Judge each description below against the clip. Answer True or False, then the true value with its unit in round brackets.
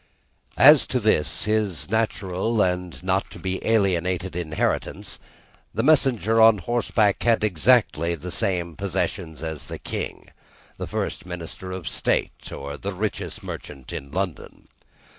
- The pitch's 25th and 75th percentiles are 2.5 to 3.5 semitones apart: False (4.2 semitones)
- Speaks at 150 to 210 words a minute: False (135 wpm)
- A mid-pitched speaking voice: False (95 Hz)